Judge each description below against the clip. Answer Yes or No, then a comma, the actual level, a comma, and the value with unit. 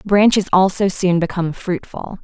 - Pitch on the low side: No, medium, 185 Hz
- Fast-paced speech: No, slow, 135 wpm